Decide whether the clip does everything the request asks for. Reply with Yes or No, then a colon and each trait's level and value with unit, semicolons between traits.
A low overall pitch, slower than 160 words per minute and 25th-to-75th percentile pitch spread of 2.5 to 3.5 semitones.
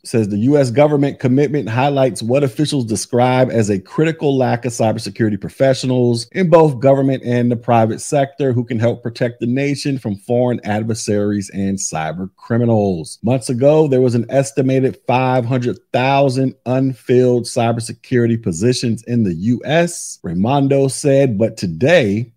Yes: low, 125 Hz; average, 140 wpm; average, 2.9 semitones